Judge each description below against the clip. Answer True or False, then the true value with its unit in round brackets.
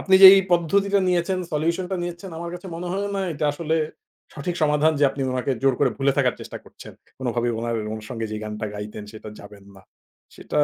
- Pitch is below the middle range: False (150 Hz)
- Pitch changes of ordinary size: False (6.8 semitones)